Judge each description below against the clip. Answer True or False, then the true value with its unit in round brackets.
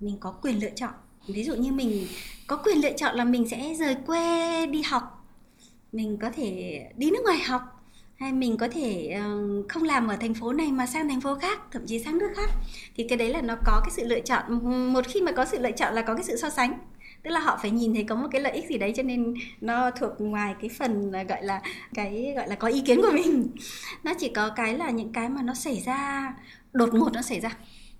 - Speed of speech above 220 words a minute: True (250 wpm)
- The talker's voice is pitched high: True (245 Hz)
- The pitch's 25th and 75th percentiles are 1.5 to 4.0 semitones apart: True (3.4 semitones)